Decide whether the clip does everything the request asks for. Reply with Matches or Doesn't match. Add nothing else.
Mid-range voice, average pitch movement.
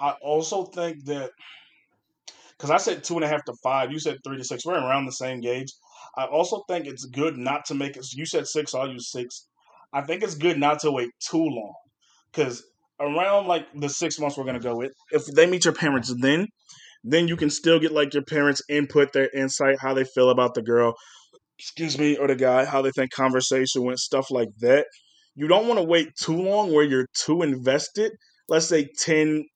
Matches